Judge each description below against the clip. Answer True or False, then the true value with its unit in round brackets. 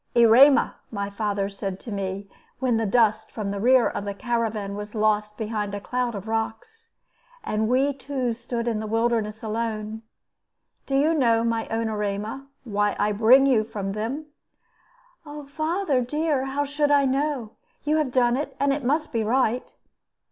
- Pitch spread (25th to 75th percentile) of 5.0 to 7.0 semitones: False (4.1 semitones)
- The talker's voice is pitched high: True (230 Hz)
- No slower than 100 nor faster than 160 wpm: False (170 wpm)